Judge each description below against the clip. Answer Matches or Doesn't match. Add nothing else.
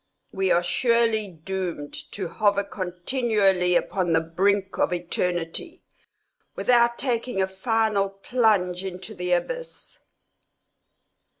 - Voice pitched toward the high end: Matches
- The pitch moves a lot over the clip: Doesn't match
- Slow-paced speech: Matches